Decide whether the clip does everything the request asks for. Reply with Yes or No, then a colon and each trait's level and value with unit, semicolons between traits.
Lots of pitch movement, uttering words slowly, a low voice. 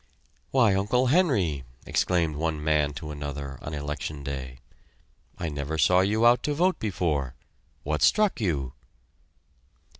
Yes: wide, 6.9 semitones; slow, 130 wpm; very low, 80 Hz